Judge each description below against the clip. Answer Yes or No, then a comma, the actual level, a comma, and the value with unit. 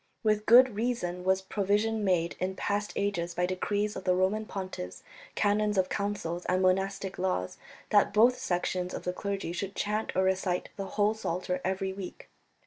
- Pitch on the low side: No, high, 195 Hz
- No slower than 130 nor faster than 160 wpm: No, average, 170 wpm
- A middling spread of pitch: No, narrow, 2.2 semitones